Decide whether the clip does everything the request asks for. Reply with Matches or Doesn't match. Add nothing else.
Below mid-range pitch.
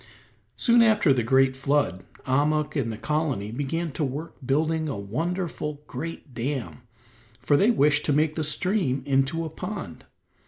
Doesn't match